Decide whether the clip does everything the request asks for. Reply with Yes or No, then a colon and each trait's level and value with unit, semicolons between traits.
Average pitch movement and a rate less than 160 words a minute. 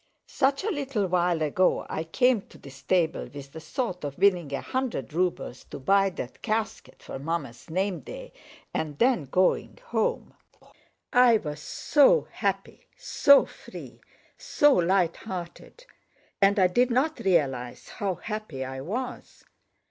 No: wide, 8.0 semitones; average, 140 wpm